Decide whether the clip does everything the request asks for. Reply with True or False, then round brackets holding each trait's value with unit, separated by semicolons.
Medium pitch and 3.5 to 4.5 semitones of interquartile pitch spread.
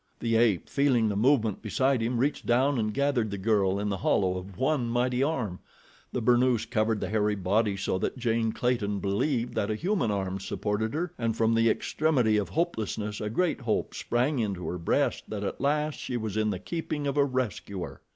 False (115 Hz; 3.9 semitones)